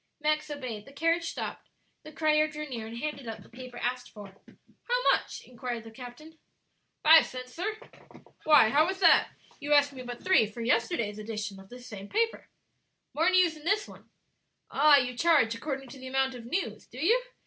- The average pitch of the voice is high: Yes, very high, 270 Hz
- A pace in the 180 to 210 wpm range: Yes, average, 190 wpm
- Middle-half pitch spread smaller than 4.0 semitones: No, average, 4.8 semitones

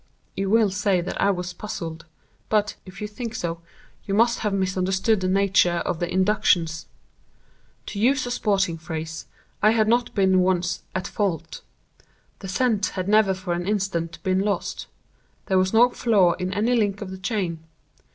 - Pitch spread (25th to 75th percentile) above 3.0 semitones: No, average, 2.7 semitones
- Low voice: No, high, 190 Hz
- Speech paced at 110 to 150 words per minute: No, average, 170 wpm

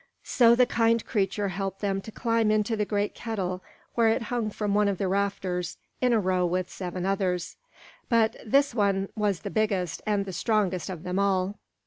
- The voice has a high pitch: Yes, high, 200 Hz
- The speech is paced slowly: No, average, 190 wpm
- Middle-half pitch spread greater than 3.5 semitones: No, average, 2.9 semitones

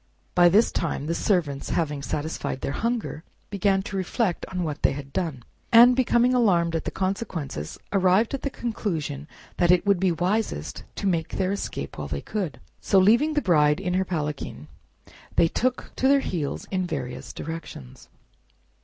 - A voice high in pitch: No, medium, 180 Hz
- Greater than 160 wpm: Yes, average, 170 wpm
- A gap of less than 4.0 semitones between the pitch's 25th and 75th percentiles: No, average, 5.2 semitones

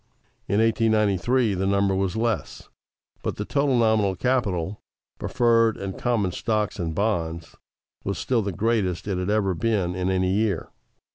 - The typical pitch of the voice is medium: No, low, 100 Hz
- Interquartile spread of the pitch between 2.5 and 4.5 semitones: Yes, average, 3.4 semitones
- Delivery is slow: No, average, 150 wpm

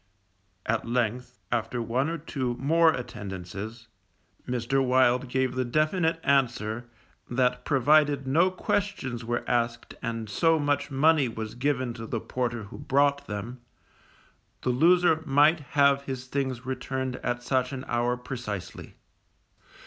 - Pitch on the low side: Yes, low, 130 Hz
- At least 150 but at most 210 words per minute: No, slow, 135 wpm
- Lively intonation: No, average, 3.0 semitones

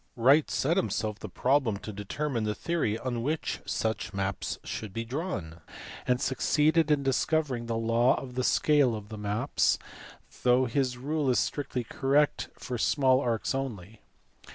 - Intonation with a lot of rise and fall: No, average, 4.3 semitones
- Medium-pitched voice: No, low, 125 Hz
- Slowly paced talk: No, average, 155 wpm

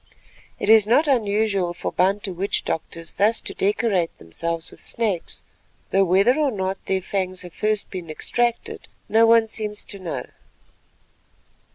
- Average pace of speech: Yes, average, 150 wpm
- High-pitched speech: Yes, high, 200 Hz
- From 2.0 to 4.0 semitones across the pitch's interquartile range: Yes, average, 3.4 semitones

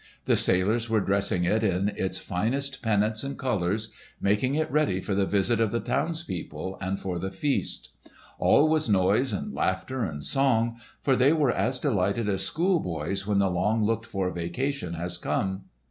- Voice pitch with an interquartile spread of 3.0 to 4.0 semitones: No, wide, 5.5 semitones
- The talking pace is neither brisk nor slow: Yes, average, 175 wpm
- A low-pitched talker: Yes, low, 105 Hz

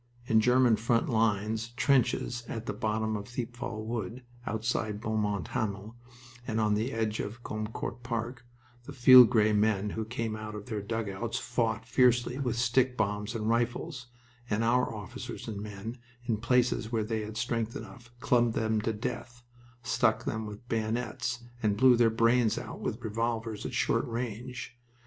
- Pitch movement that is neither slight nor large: No, narrow, 2.0 semitones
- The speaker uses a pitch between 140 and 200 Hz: No, low, 115 Hz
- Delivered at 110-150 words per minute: No, average, 165 wpm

